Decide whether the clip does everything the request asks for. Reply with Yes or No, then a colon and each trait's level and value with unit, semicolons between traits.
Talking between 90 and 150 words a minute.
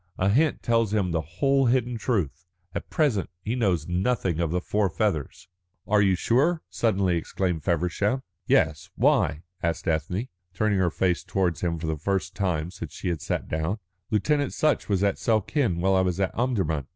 No: average, 180 wpm